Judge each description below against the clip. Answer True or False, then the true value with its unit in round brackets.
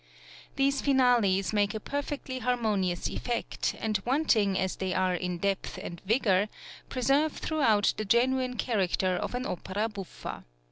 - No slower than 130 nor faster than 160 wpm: True (140 wpm)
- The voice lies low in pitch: False (215 Hz)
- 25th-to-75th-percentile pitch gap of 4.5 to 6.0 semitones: True (5.1 semitones)